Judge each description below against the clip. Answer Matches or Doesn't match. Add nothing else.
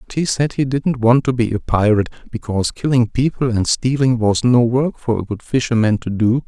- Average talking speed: Doesn't match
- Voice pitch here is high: Doesn't match